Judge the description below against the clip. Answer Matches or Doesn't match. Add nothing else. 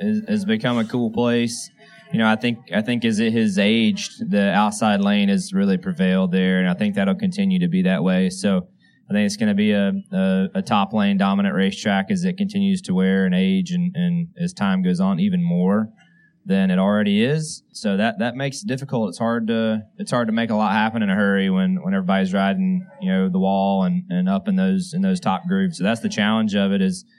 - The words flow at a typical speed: Doesn't match